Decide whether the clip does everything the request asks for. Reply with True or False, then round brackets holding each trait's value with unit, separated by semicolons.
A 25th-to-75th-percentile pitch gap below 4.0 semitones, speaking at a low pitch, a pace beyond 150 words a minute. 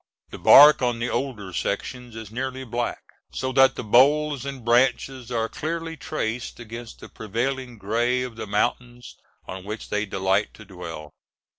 True (3.3 semitones; 120 Hz; 160 wpm)